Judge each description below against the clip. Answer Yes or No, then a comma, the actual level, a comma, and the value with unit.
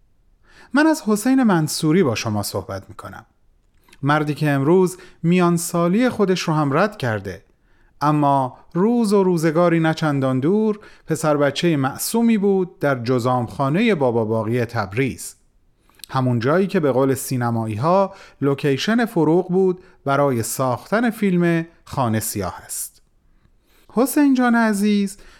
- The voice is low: No, medium, 155 Hz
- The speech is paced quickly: No, average, 130 wpm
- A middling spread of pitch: No, wide, 7.1 semitones